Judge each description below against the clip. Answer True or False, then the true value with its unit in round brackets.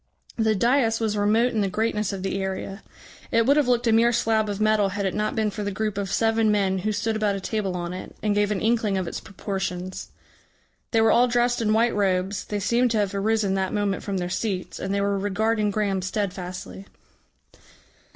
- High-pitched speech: True (205 Hz)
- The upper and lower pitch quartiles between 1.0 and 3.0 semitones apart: True (2.5 semitones)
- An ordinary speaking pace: False (220 wpm)